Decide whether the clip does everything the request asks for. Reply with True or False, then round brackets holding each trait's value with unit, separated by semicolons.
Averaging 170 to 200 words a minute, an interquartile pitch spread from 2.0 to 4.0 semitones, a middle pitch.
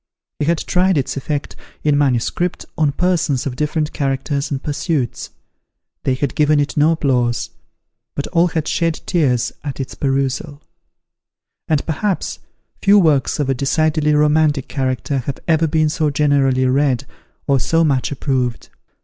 False (150 wpm; 2.8 semitones; 145 Hz)